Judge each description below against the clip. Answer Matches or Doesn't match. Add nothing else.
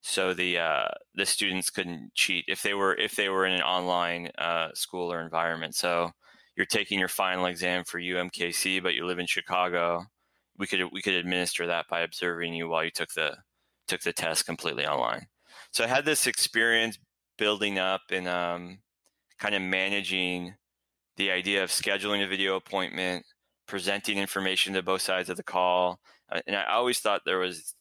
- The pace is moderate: Matches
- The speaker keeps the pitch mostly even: Matches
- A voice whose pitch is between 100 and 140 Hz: Doesn't match